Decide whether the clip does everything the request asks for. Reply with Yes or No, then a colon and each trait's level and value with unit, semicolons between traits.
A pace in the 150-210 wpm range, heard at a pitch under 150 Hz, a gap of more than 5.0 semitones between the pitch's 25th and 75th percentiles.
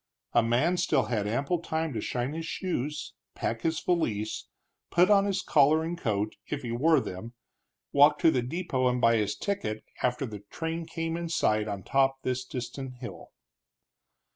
Yes: average, 180 wpm; low, 135 Hz; wide, 5.6 semitones